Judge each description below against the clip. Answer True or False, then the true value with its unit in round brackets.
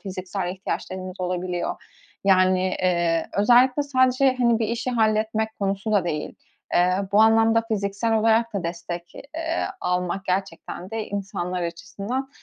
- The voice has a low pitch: False (200 Hz)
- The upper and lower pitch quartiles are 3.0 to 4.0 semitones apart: True (3.7 semitones)